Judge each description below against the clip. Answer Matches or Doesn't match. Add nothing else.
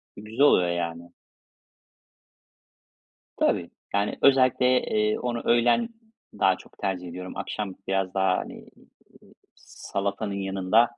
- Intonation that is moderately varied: Matches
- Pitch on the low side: Matches